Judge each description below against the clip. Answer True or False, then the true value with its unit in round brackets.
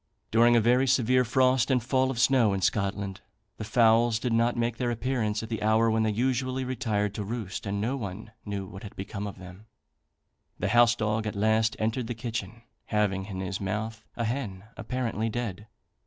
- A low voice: True (110 Hz)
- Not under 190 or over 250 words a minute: True (195 wpm)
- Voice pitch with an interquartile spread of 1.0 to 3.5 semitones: True (2.5 semitones)